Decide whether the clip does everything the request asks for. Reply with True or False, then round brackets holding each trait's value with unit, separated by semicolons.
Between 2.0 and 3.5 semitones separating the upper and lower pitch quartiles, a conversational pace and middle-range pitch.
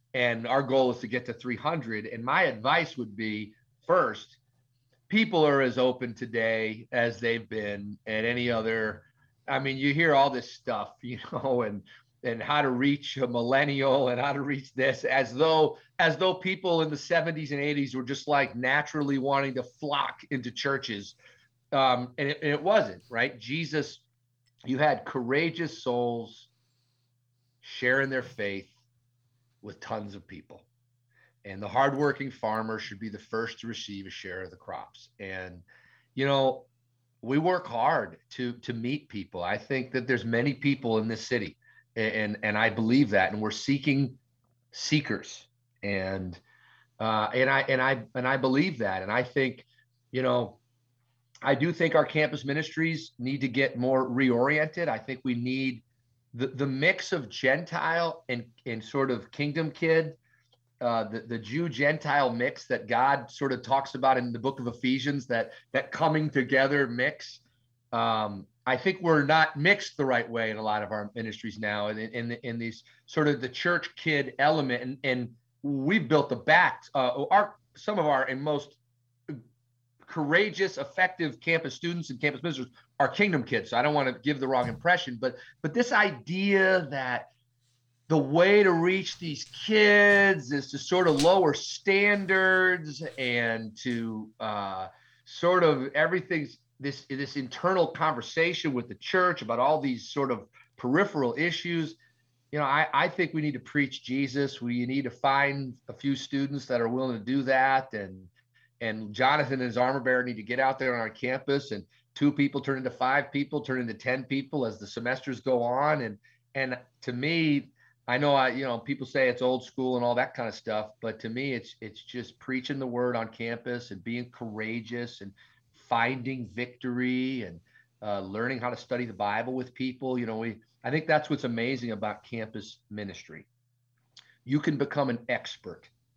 False (3.2 semitones; 180 wpm; 125 Hz)